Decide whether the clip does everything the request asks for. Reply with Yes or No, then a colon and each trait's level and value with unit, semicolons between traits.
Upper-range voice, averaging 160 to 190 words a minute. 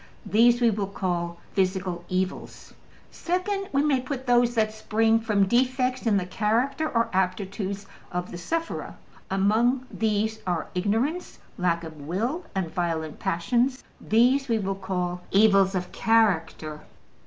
No: high, 210 Hz; average, 140 wpm